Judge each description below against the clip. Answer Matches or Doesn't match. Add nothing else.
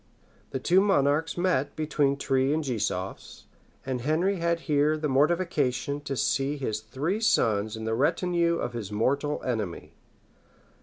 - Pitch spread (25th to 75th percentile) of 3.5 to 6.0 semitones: Matches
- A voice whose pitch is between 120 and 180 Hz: Matches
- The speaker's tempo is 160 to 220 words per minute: Doesn't match